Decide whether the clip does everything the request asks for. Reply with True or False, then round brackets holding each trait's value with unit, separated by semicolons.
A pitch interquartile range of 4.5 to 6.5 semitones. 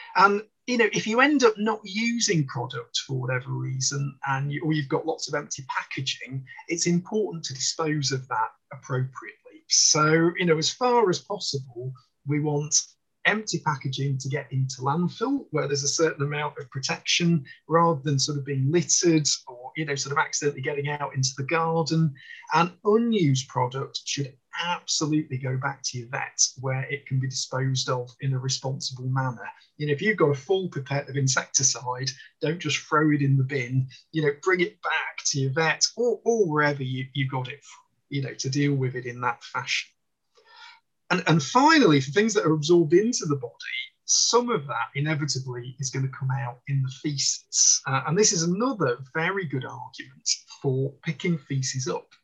False (4.1 semitones)